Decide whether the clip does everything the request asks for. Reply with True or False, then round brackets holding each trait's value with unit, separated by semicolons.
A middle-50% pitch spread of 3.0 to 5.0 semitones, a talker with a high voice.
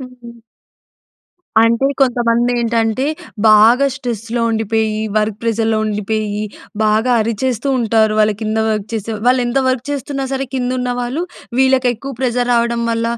False (2.5 semitones; 235 Hz)